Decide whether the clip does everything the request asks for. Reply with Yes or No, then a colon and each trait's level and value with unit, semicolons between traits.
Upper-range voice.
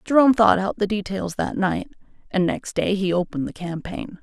Yes: high, 195 Hz